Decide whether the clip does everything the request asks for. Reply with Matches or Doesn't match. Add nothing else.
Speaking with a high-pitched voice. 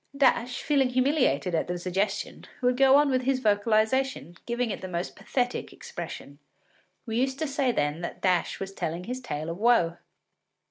Matches